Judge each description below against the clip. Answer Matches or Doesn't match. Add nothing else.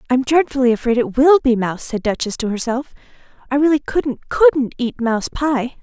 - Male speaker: Doesn't match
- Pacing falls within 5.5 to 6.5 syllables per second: Matches